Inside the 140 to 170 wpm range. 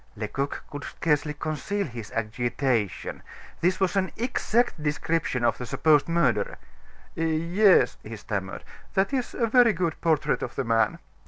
Yes: average, 145 wpm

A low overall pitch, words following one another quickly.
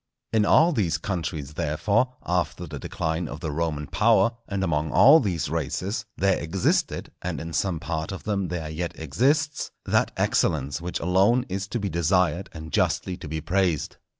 No: very low, 90 Hz; average, 175 wpm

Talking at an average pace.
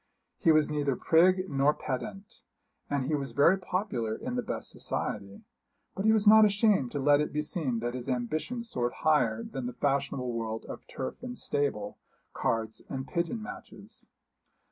Yes: average, 170 wpm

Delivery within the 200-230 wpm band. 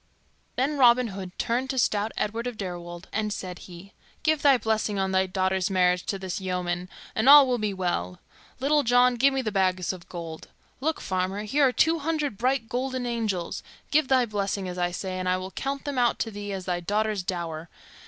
Yes: fast, 205 wpm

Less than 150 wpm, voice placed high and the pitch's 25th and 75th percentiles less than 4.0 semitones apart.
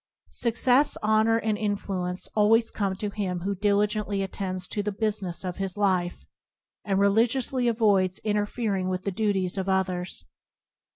Yes: average, 140 wpm; high, 200 Hz; narrow, 2.5 semitones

